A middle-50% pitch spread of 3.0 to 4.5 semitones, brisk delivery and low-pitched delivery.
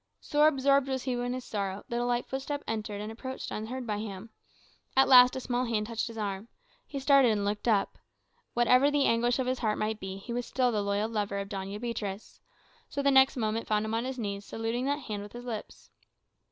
No: average, 3.5 semitones; fast, 220 wpm; high, 230 Hz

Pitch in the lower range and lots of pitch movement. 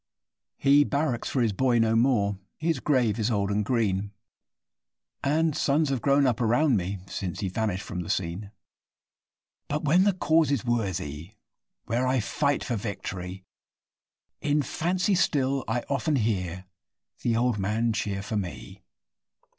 Yes: low, 115 Hz; wide, 5.7 semitones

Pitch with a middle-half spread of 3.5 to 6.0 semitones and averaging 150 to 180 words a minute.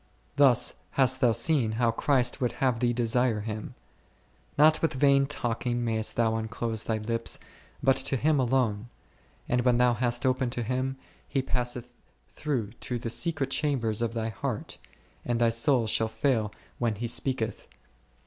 No: narrow, 2.5 semitones; average, 160 wpm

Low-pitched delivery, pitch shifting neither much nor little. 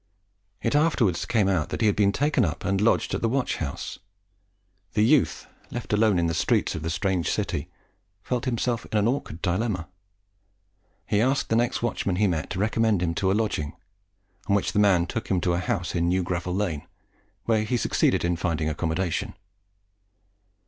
Yes: low, 100 Hz; average, 4.7 semitones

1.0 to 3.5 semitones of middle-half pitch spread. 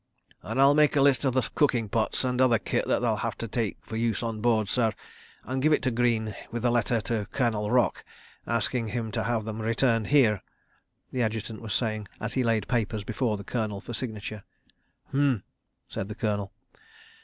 Yes: narrow, 2.5 semitones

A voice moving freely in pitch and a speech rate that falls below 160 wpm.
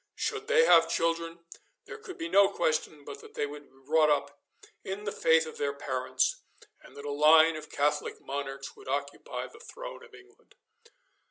No: wide, 6.7 semitones; average, 185 wpm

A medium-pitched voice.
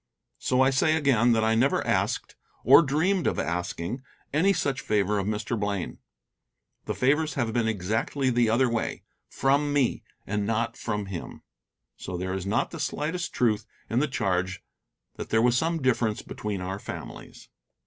No: low, 115 Hz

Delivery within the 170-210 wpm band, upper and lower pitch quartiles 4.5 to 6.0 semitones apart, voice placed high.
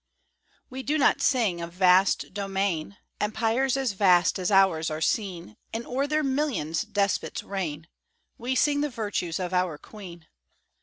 No: average, 150 wpm; wide, 5.6 semitones; high, 200 Hz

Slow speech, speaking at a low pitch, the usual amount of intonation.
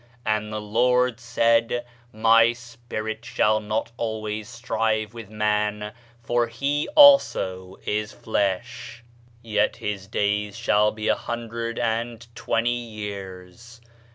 No: slow, 120 wpm; low, 110 Hz; narrow, 1.9 semitones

